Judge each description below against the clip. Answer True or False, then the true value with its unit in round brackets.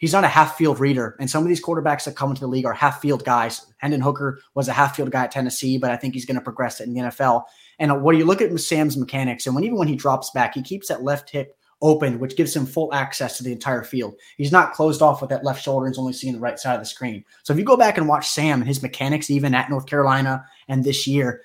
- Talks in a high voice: False (140 Hz)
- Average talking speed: False (285 wpm)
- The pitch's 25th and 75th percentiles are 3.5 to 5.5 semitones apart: False (2.6 semitones)